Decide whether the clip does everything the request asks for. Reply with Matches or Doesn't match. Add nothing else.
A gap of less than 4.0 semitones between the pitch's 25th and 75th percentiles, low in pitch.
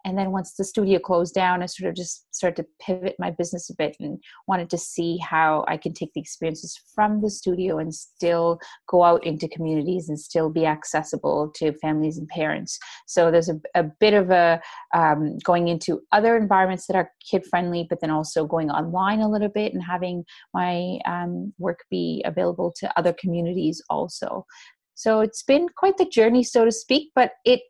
Doesn't match